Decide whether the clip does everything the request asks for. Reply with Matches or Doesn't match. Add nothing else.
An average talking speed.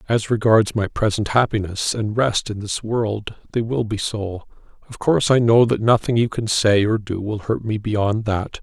Doesn't match